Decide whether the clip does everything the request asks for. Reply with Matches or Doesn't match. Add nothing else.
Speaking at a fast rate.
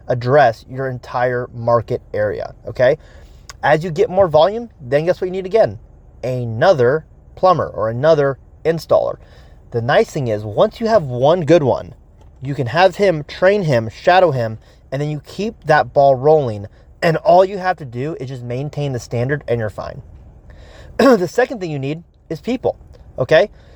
Doesn't match